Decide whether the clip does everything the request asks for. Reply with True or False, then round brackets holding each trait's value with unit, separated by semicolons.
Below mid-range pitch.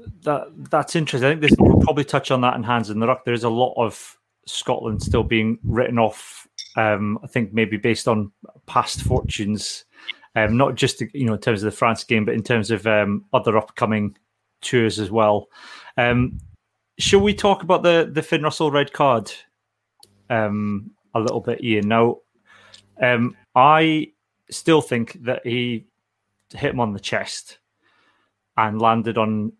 True (115 Hz)